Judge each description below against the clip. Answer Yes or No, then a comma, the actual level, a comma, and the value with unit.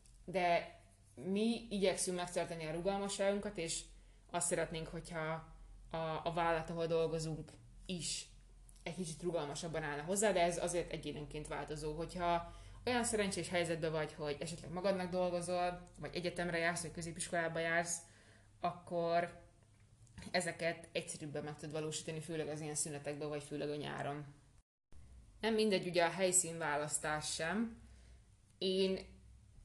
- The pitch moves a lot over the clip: No, average, 2.9 semitones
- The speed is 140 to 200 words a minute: No, average, 125 wpm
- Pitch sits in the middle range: Yes, medium, 165 Hz